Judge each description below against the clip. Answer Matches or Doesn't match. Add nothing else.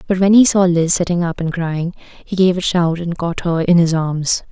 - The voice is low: Doesn't match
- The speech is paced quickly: Matches